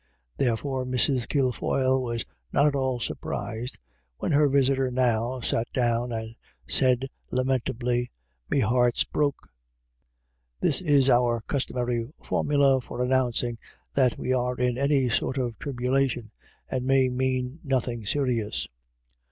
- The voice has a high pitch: No, low, 125 Hz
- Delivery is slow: Yes, slow, 130 wpm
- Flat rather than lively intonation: Yes, narrow, 1.9 semitones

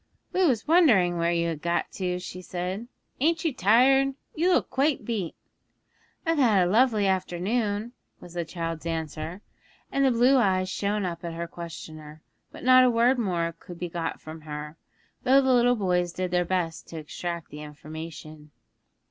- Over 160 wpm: Yes, average, 175 wpm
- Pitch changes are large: Yes, wide, 6.3 semitones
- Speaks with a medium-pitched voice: Yes, medium, 180 Hz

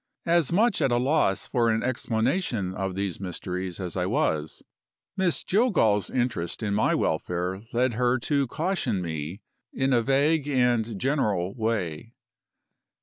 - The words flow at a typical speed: Yes, average, 145 wpm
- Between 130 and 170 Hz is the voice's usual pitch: No, low, 115 Hz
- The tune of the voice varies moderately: No, wide, 6.3 semitones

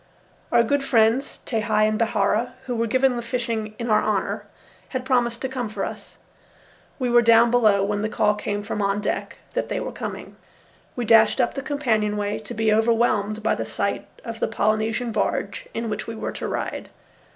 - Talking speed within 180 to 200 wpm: Yes, average, 195 wpm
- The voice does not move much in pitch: Yes, narrow, 2.1 semitones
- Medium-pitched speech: No, high, 225 Hz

